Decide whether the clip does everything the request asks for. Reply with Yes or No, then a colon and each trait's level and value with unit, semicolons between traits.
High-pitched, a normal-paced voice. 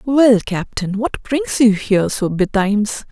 Yes: high, 220 Hz; average, 155 wpm